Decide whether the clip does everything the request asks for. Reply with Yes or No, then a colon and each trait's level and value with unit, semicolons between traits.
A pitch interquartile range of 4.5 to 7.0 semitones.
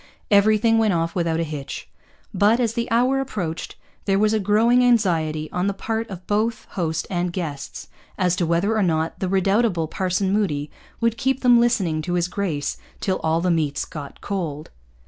Yes: average, 4.9 semitones